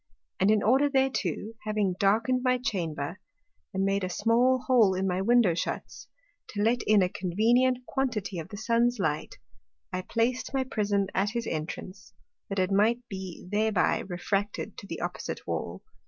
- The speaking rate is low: No, average, 165 wpm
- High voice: Yes, high, 210 Hz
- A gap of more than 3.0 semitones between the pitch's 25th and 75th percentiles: Yes, average, 4.2 semitones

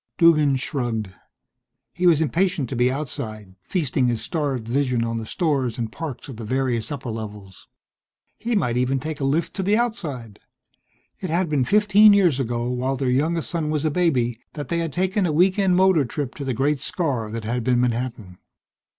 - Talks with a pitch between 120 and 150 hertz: Yes, low, 135 Hz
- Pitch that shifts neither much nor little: No, wide, 5.7 semitones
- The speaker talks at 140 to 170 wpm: No, average, 190 wpm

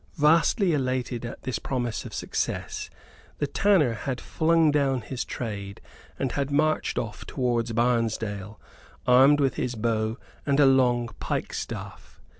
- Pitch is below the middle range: Yes, low, 125 Hz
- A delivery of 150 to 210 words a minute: No, average, 140 wpm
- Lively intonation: No, average, 3.6 semitones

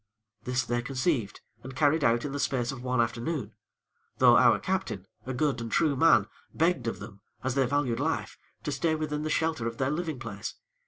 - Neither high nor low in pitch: No, low, 130 Hz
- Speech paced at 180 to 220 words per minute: Yes, average, 200 wpm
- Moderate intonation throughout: Yes, average, 4.2 semitones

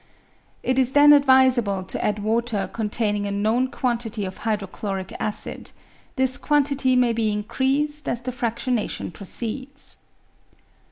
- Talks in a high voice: Yes, high, 235 Hz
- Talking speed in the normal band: No, slow, 120 wpm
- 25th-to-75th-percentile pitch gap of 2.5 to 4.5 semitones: Yes, average, 3.8 semitones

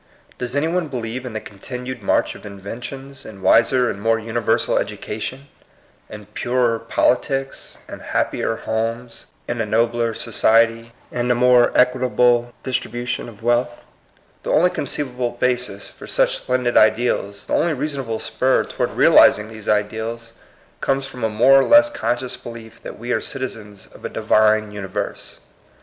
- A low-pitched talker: Yes, low, 120 Hz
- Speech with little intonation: Yes, narrow, 2.3 semitones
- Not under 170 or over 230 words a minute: No, average, 155 wpm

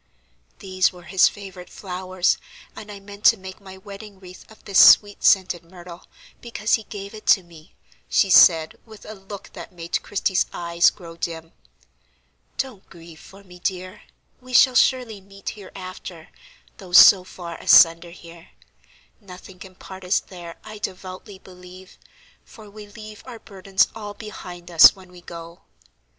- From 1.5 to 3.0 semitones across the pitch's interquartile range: Yes, narrow, 2.5 semitones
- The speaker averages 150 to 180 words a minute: Yes, average, 160 wpm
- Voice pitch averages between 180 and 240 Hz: Yes, high, 190 Hz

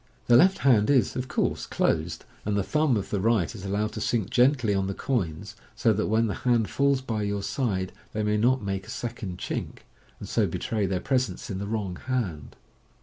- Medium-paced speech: No, fast, 210 wpm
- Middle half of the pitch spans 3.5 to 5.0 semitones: Yes, average, 4.0 semitones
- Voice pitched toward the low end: Yes, low, 110 Hz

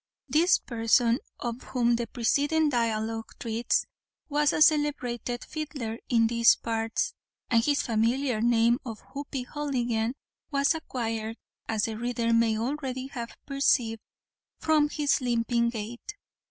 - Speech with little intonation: No, average, 3.6 semitones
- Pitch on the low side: No, high, 240 Hz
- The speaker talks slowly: Yes, slow, 125 wpm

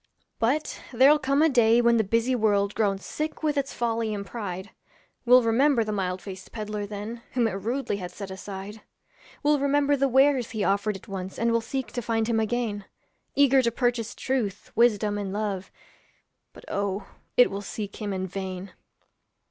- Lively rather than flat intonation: No, average, 3.6 semitones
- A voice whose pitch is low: No, high, 220 Hz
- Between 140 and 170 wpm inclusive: No, average, 180 wpm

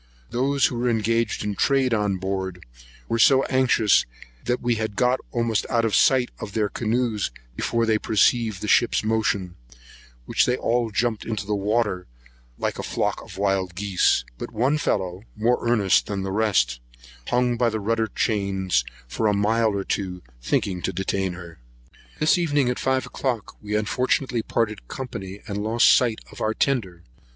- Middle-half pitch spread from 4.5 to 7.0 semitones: No, average, 3.5 semitones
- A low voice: Yes, low, 110 Hz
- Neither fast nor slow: Yes, average, 170 wpm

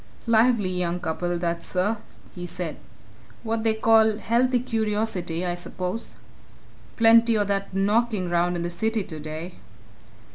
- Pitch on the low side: No, high, 195 Hz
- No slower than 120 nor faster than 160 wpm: Yes, slow, 135 wpm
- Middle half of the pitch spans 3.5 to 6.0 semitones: Yes, average, 4.2 semitones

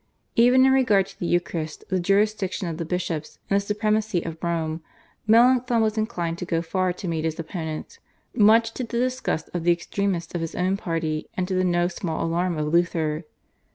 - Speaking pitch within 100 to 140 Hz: No, medium, 180 Hz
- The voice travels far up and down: No, average, 4.4 semitones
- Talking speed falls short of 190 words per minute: No, average, 195 wpm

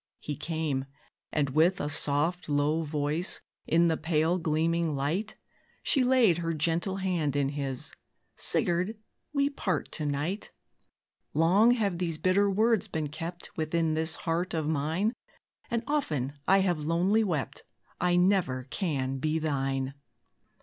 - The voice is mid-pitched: Yes, medium, 165 Hz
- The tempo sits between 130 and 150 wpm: Yes, average, 140 wpm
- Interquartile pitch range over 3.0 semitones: Yes, average, 3.8 semitones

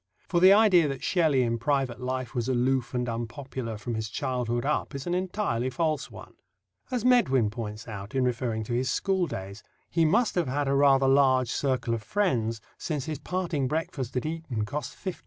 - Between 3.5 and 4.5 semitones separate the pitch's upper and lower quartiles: No, average, 5.1 semitones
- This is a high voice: No, low, 130 Hz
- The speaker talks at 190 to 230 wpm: Yes, average, 195 wpm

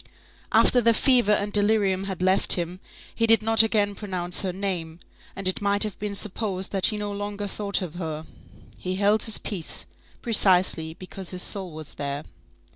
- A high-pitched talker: Yes, high, 195 Hz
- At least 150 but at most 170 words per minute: No, average, 180 wpm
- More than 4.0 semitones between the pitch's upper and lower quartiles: No, narrow, 2.4 semitones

